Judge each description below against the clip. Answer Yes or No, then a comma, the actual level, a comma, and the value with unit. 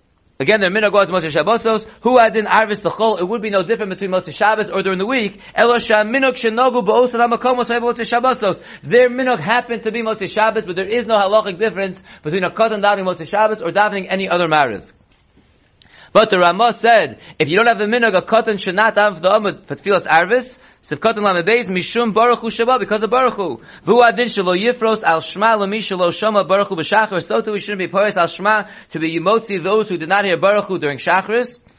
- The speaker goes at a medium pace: Yes, average, 195 wpm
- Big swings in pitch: No, average, 3.2 semitones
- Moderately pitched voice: No, high, 215 Hz